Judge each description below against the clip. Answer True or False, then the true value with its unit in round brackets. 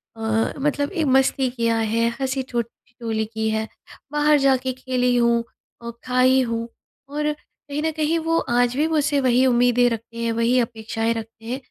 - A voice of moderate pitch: False (245 Hz)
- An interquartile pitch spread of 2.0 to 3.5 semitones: True (2.9 semitones)